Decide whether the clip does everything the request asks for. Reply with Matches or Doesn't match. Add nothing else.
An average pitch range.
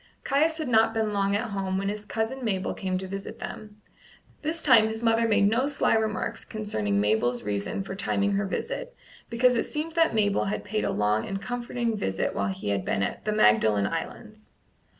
Matches